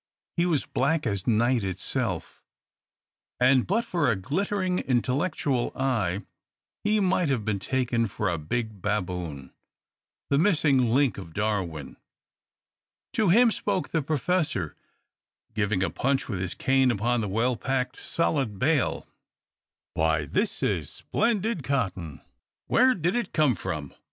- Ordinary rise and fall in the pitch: No, wide, 8.0 semitones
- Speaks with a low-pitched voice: Yes, low, 125 Hz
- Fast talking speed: No, slow, 135 wpm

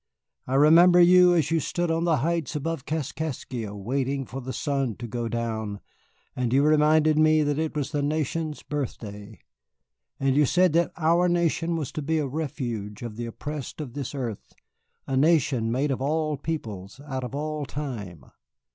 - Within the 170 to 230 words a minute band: Yes, average, 175 wpm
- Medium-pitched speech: Yes, medium, 145 Hz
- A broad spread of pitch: No, average, 4.2 semitones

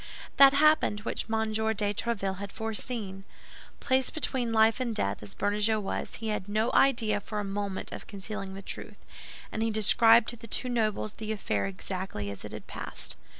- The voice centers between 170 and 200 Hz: No, high, 215 Hz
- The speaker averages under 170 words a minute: No, average, 185 wpm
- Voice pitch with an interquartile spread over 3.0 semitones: No, narrow, 2.4 semitones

